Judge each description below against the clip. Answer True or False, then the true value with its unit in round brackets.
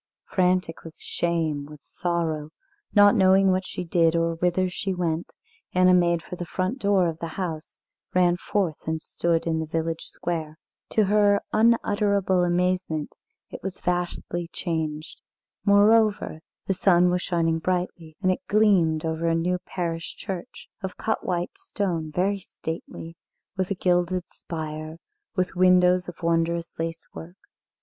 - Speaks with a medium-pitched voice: True (175 Hz)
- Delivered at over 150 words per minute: False (145 wpm)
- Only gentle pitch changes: True (2.3 semitones)